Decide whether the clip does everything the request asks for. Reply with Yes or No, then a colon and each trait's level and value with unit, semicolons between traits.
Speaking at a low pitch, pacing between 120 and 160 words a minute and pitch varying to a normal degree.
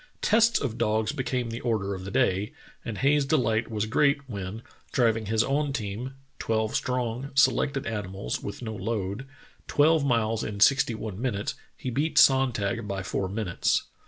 No: low, 115 Hz; average, 170 wpm; average, 4.3 semitones